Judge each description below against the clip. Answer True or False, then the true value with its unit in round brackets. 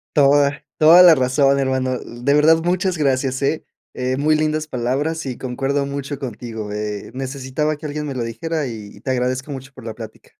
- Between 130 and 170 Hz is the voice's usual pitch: True (135 Hz)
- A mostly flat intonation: False (3.0 semitones)